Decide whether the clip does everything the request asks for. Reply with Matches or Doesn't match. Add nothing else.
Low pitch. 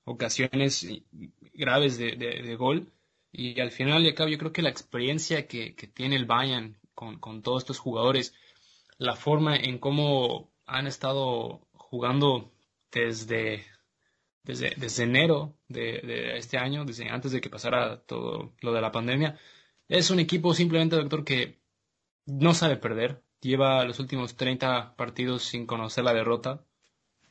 Matches